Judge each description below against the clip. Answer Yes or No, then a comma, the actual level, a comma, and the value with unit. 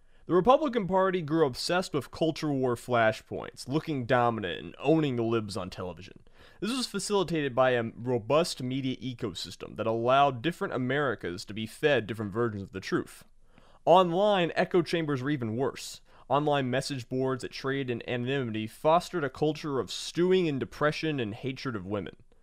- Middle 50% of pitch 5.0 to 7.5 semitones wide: Yes, wide, 5.5 semitones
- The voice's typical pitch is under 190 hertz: Yes, low, 135 Hz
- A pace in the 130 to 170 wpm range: Yes, average, 165 wpm